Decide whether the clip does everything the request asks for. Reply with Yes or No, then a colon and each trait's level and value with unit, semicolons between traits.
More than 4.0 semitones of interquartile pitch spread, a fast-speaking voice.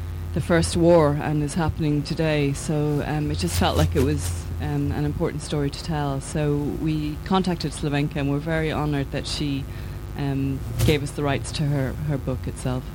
No: average, 4.8 semitones; average, 190 wpm